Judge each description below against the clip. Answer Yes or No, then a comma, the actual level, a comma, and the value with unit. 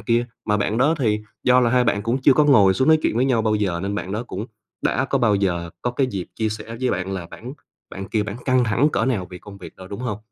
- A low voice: Yes, low, 110 Hz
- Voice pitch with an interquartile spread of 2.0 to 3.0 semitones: No, average, 4.0 semitones